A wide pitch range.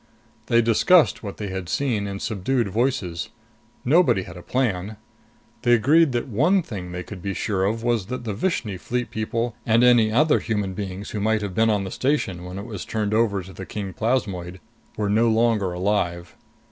No: average, 3.8 semitones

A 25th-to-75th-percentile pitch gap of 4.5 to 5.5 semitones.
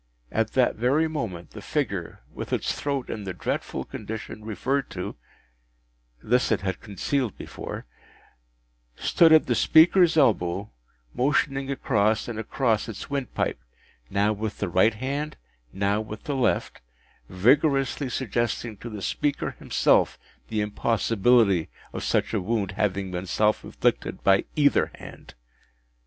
Yes: average, 5.2 semitones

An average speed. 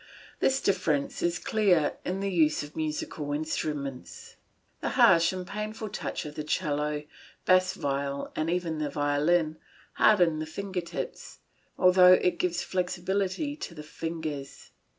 Yes: average, 145 wpm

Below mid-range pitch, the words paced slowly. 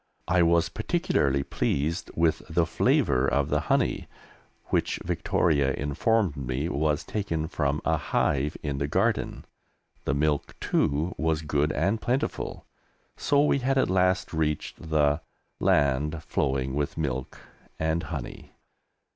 Yes: very low, 75 Hz; slow, 130 wpm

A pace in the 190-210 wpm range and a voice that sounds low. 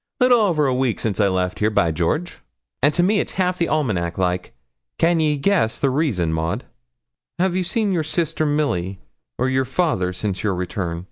Yes: average, 195 wpm; low, 130 Hz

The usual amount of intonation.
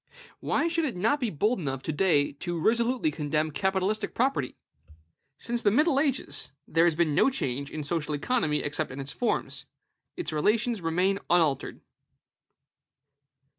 No: wide, 7.9 semitones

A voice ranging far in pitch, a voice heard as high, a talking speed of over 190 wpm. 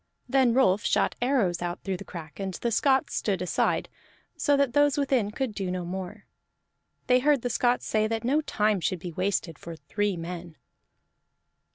No: wide, 5.8 semitones; high, 205 Hz; average, 180 wpm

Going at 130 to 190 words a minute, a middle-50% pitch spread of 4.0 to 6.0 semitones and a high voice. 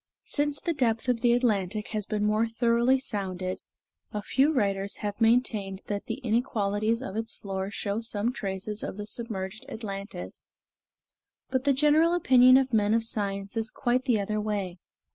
No: average, 165 wpm; average, 3.4 semitones; high, 220 Hz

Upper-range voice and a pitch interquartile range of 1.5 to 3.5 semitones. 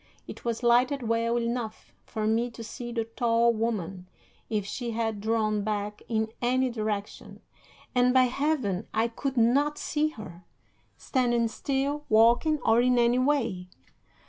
Yes: high, 235 Hz; narrow, 2.4 semitones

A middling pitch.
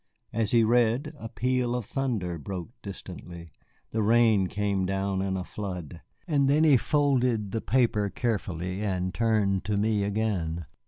No: low, 105 Hz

